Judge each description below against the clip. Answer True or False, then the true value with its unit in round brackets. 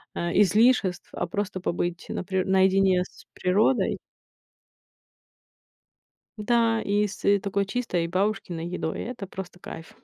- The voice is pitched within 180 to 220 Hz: True (190 Hz)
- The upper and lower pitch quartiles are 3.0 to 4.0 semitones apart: False (2.4 semitones)